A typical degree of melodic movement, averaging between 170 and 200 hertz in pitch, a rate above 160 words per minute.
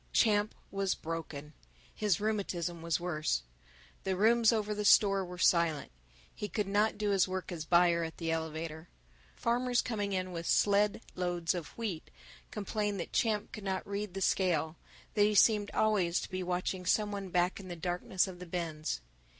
Yes: average, 3.5 semitones; medium, 185 Hz; average, 175 wpm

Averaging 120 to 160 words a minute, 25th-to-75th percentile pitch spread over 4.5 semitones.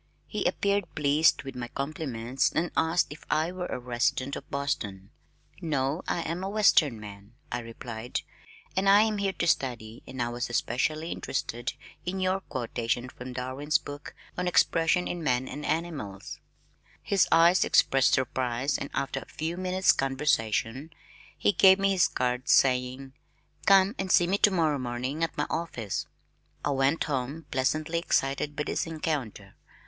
Yes: average, 155 wpm; average, 5.3 semitones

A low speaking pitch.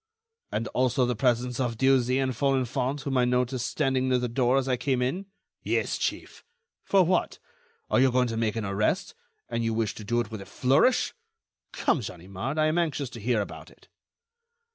Yes: low, 125 Hz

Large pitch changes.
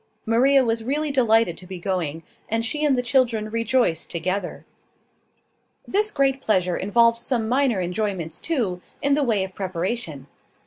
Yes: wide, 5.9 semitones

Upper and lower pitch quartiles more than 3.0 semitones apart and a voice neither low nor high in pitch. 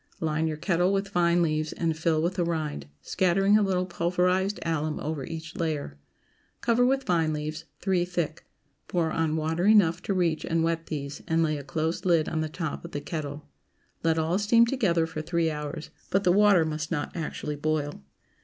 No: narrow, 2.5 semitones; medium, 165 Hz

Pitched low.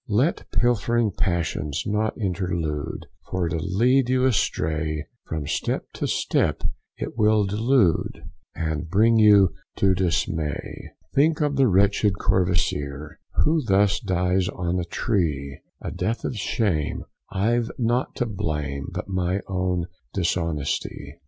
Yes: very low, 95 Hz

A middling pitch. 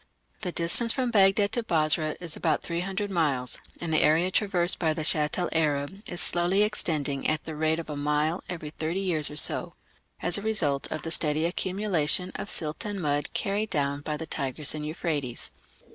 Yes: medium, 165 Hz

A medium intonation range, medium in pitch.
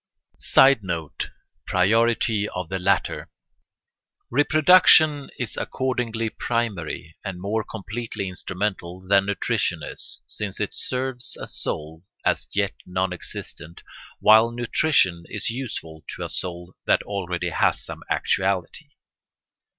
No: average, 4.6 semitones; low, 100 Hz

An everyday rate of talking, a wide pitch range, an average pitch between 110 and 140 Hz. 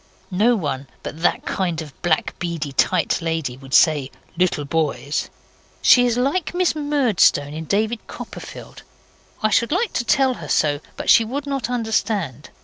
No: average, 160 wpm; wide, 8.2 semitones; medium, 185 Hz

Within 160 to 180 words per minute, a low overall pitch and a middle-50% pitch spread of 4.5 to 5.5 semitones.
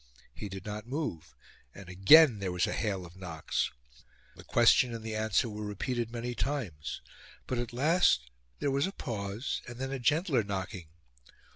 Yes: average, 170 wpm; low, 110 Hz; average, 5.0 semitones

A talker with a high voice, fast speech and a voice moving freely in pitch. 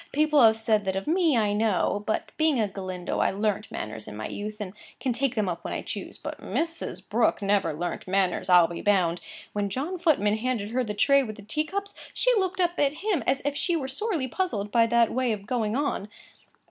Yes: high, 225 Hz; fast, 225 wpm; wide, 6.4 semitones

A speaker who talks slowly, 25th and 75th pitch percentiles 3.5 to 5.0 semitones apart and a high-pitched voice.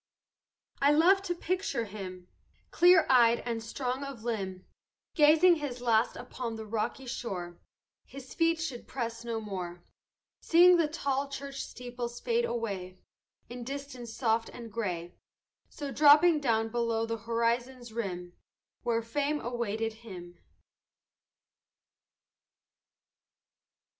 Yes: slow, 120 wpm; average, 4.0 semitones; high, 240 Hz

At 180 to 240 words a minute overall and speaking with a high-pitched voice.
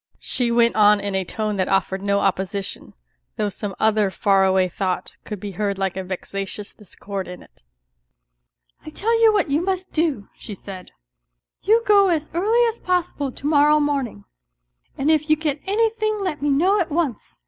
Yes: average, 185 wpm; high, 235 Hz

